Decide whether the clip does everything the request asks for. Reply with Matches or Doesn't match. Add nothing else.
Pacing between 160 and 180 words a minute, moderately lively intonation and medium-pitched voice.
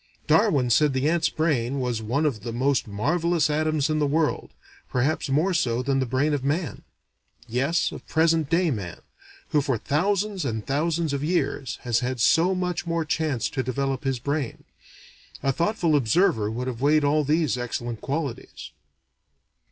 Matches